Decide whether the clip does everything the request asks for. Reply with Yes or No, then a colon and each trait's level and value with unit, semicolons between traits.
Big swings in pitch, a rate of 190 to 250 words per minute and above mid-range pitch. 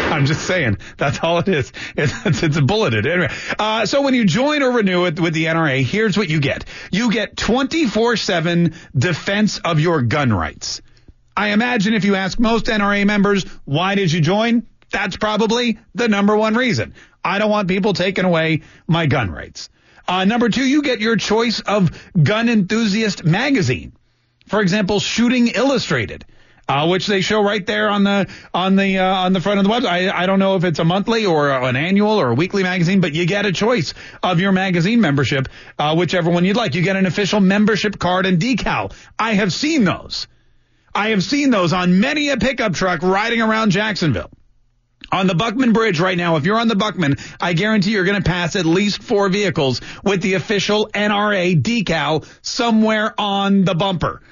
No: average, 3.9 semitones; average, 195 wpm; high, 195 Hz